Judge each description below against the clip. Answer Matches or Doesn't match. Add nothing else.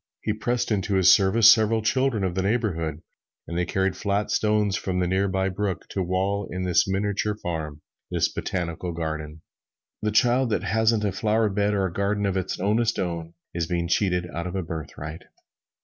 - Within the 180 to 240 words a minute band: Matches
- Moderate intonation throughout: Matches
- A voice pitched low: Matches